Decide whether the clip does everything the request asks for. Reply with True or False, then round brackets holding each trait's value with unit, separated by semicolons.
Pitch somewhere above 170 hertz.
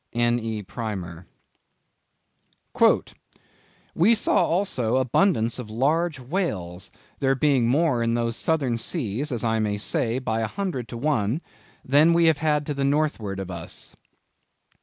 False (125 Hz)